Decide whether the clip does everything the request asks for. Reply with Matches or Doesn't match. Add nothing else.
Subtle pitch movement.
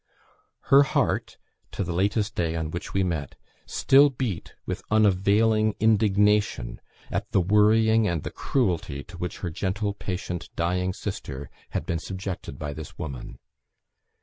Doesn't match